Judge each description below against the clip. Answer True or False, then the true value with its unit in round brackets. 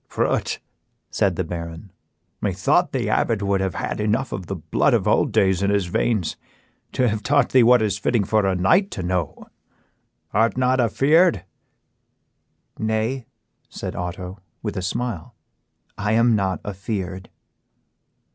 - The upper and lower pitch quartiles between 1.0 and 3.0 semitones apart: False (3.7 semitones)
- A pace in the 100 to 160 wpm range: True (145 wpm)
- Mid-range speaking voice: False (100 Hz)